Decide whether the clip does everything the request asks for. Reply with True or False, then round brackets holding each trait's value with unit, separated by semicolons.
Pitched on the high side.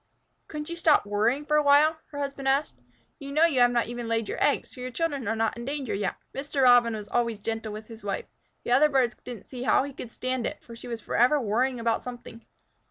True (245 Hz)